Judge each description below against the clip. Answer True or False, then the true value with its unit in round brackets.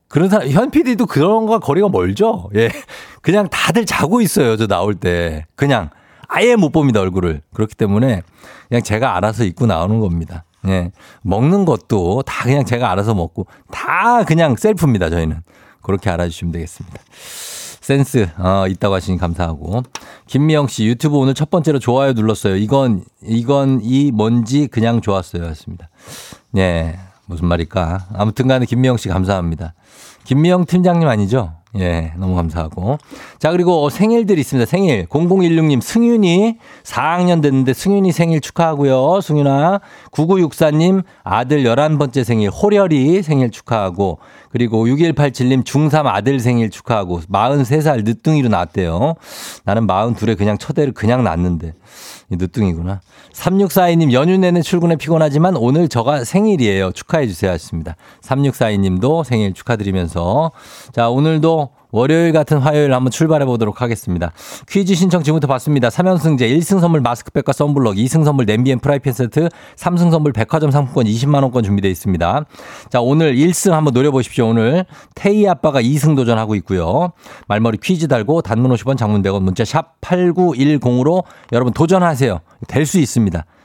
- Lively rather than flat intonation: True (7.6 semitones)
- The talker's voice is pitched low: True (130 Hz)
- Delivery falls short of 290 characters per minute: False (335 characters per minute)